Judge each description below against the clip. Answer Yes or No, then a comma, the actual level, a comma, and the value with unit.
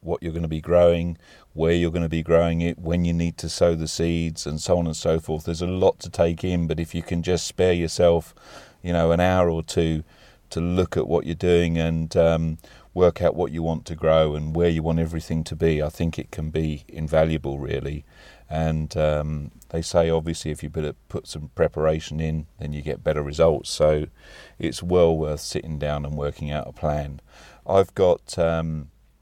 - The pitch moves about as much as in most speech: No, narrow, 1.6 semitones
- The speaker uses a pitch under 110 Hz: Yes, very low, 80 Hz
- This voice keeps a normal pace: No, fast, 215 wpm